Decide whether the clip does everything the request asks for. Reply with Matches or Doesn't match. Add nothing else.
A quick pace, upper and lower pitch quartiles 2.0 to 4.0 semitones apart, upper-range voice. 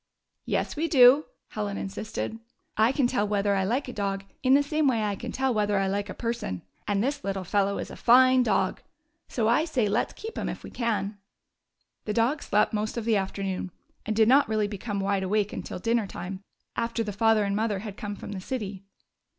Matches